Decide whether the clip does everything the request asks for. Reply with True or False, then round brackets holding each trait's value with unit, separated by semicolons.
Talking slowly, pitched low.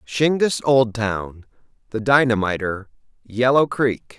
True (70 wpm; 120 Hz)